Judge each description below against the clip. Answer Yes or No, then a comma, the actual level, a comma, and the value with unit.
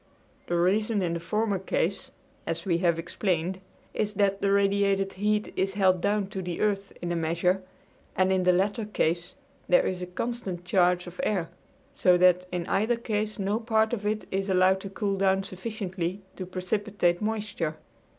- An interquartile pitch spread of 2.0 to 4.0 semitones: Yes, narrow, 2.6 semitones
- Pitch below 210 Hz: Yes, high, 190 Hz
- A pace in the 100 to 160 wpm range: No, average, 180 wpm